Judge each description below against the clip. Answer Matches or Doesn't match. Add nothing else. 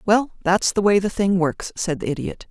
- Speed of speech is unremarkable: Doesn't match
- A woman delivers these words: Matches